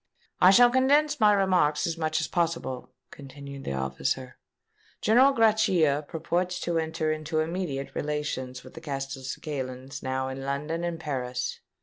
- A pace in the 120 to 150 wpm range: Yes, average, 140 wpm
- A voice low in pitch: No, medium, 155 Hz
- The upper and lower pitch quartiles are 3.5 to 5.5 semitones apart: Yes, average, 4.6 semitones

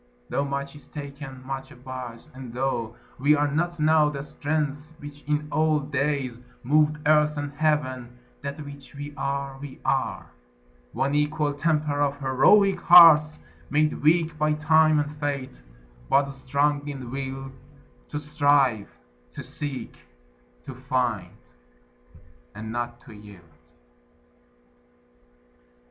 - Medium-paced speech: No, slow, 125 wpm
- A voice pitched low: No, medium, 145 Hz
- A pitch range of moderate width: No, narrow, 2.2 semitones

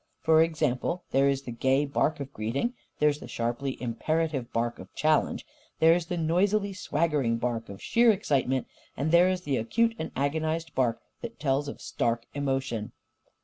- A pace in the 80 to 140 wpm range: No, average, 175 wpm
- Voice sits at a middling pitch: Yes, medium, 145 Hz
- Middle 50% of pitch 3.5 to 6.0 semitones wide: Yes, average, 4.7 semitones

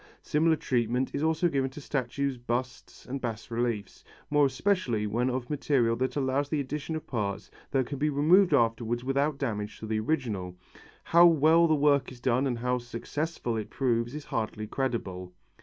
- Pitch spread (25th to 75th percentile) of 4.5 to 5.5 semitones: No, average, 3.9 semitones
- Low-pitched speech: Yes, low, 130 Hz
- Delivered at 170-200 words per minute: Yes, average, 175 wpm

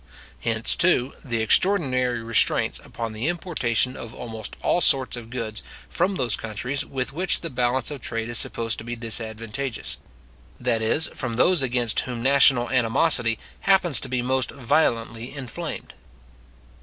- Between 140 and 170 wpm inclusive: Yes, average, 150 wpm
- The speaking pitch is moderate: No, low, 125 Hz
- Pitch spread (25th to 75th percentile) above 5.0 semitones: No, average, 3.1 semitones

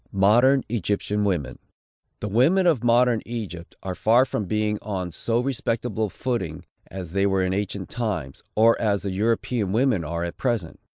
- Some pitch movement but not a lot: Yes, average, 4.0 semitones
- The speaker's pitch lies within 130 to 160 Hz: No, low, 105 Hz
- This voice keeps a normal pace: Yes, average, 170 wpm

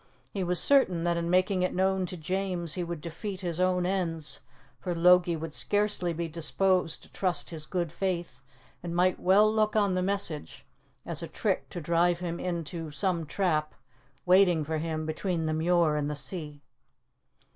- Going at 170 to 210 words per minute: Yes, average, 180 wpm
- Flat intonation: Yes, narrow, 2.3 semitones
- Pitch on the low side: No, medium, 175 Hz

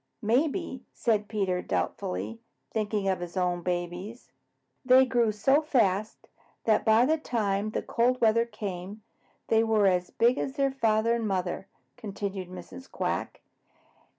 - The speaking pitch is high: Yes, high, 215 Hz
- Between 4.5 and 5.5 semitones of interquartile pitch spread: No, average, 4.1 semitones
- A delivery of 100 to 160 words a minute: Yes, average, 140 wpm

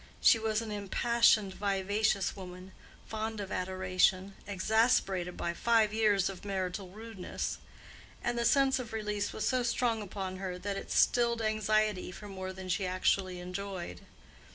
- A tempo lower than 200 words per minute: Yes, average, 150 wpm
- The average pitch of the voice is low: No, high, 200 Hz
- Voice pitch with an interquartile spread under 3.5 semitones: Yes, average, 2.8 semitones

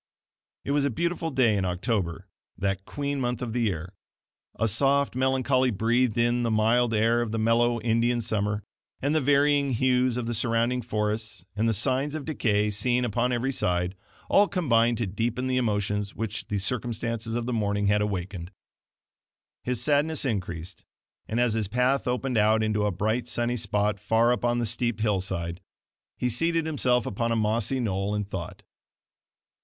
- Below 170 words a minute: No, average, 175 wpm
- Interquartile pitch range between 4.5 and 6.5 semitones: No, average, 3.2 semitones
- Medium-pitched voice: No, low, 115 Hz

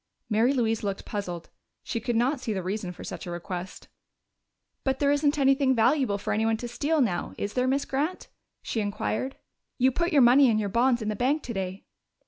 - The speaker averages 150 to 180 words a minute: No, average, 200 wpm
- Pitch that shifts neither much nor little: Yes, average, 4.7 semitones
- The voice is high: Yes, high, 235 Hz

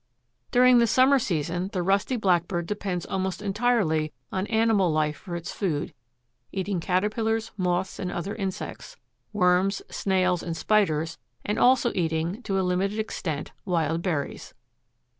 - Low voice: No, high, 190 Hz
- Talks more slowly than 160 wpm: Yes, slow, 135 wpm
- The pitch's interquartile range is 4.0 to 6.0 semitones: No, average, 3.5 semitones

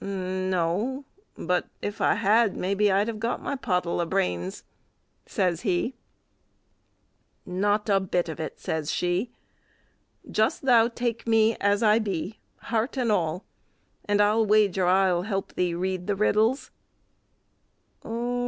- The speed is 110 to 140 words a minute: Yes, slow, 135 wpm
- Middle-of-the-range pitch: No, high, 200 Hz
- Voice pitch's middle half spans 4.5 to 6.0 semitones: No, average, 3.5 semitones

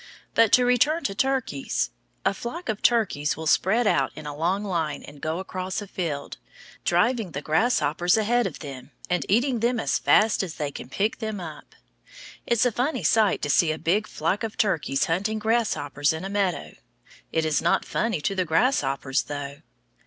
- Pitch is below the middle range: No, high, 190 Hz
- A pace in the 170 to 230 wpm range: Yes, average, 190 wpm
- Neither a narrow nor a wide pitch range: No, wide, 6.4 semitones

